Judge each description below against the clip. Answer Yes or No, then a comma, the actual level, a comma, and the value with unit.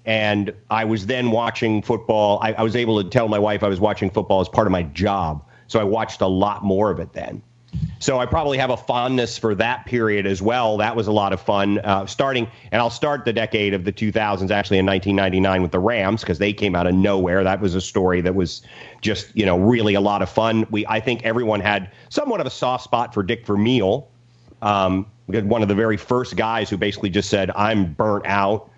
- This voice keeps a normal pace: No, fast, 240 wpm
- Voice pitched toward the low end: Yes, low, 105 Hz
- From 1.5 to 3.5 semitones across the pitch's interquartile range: Yes, narrow, 2.5 semitones